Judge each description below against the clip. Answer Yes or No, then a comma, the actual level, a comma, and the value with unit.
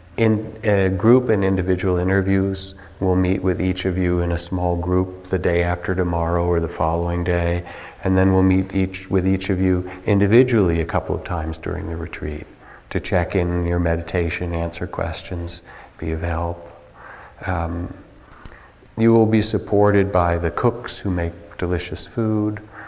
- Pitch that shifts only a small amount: Yes, narrow, 2.0 semitones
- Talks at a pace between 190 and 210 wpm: No, average, 165 wpm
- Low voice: Yes, very low, 90 Hz